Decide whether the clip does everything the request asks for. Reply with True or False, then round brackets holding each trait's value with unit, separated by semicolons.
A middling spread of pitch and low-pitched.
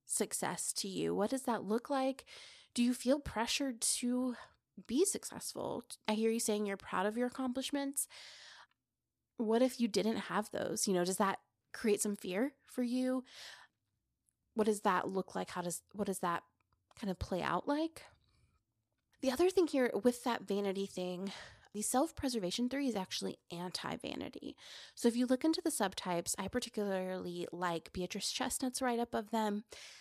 False (4.7 semitones; 225 Hz)